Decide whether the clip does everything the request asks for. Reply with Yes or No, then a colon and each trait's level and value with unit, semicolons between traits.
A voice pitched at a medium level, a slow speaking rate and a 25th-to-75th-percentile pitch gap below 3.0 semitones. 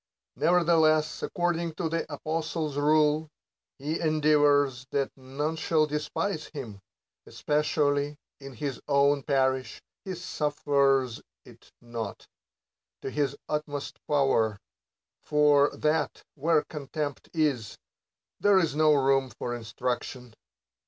Yes: medium, 145 Hz; slow, 110 wpm; narrow, 2.4 semitones